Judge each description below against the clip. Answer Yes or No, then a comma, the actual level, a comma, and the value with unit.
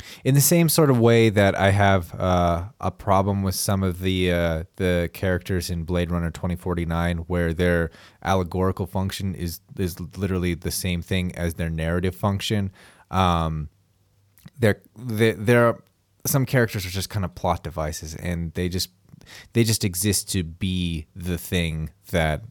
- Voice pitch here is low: Yes, very low, 95 Hz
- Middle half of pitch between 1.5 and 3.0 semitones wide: Yes, narrow, 2.5 semitones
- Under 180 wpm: Yes, average, 165 wpm